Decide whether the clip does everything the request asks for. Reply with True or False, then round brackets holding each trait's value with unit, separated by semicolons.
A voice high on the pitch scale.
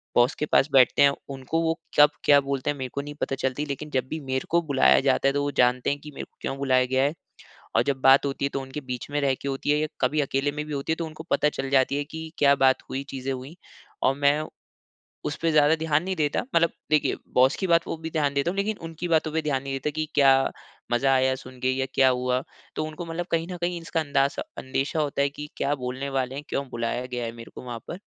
False (140 Hz)